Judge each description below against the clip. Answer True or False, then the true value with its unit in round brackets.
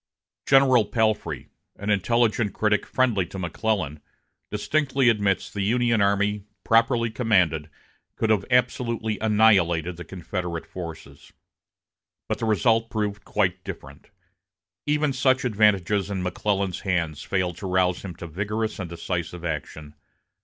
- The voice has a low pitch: True (100 Hz)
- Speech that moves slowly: True (130 wpm)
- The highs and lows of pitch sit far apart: False (3.9 semitones)